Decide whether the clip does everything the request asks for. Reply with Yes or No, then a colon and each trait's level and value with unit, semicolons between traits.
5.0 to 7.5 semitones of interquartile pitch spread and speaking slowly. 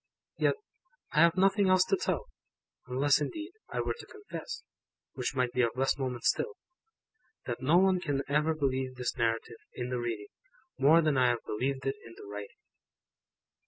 No: wide, 5.4 semitones; average, 175 wpm